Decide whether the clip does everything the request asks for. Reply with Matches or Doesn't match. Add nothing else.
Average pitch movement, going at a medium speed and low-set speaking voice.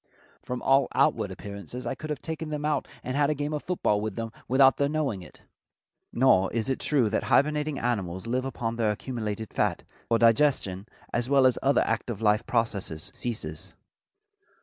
Matches